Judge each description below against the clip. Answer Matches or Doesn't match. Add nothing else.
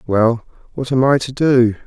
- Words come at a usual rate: Matches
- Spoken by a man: Matches